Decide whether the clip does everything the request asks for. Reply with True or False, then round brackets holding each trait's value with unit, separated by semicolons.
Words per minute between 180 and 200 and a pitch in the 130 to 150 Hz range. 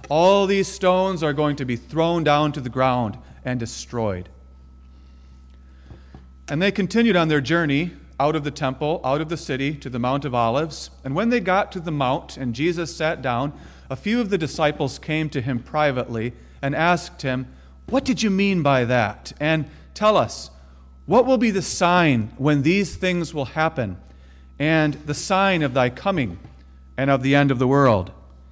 True (185 wpm; 140 Hz)